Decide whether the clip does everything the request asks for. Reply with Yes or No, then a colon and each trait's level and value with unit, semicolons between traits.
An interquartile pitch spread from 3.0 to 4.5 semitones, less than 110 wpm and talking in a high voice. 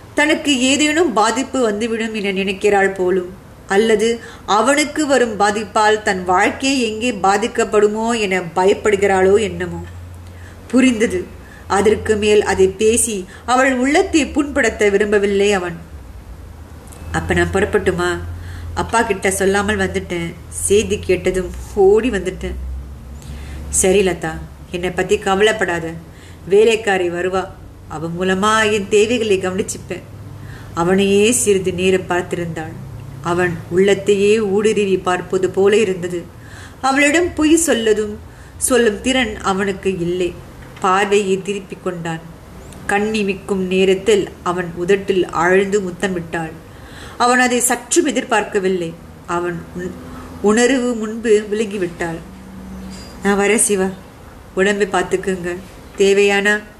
Yes: average, 3.4 semitones; average, 100 wpm; high, 195 Hz